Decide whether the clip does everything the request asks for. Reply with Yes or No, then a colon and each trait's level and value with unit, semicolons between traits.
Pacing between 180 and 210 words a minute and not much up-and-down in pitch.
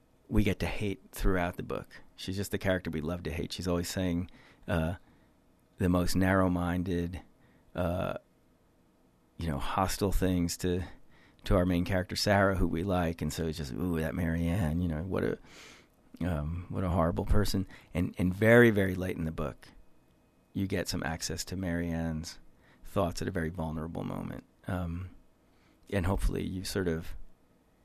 No: average, 170 wpm; narrow, 2.1 semitones